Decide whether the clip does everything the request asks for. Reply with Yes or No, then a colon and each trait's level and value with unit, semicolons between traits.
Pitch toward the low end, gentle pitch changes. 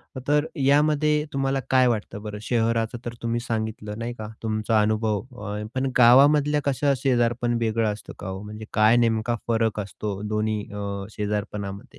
No: low, 110 Hz; average, 3.0 semitones